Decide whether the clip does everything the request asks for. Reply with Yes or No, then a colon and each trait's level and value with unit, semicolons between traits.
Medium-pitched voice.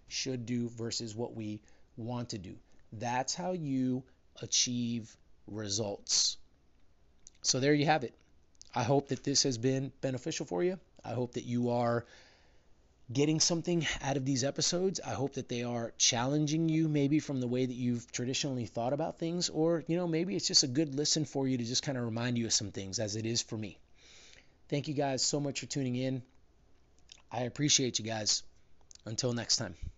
No: low, 125 Hz